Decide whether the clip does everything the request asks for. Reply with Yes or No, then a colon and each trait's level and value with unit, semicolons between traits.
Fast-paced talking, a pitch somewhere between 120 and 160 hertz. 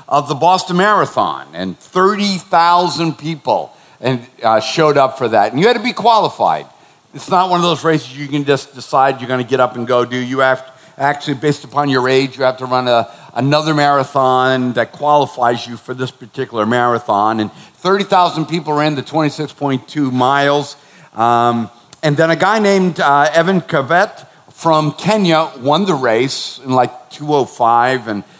No: average, 190 wpm; medium, 140 Hz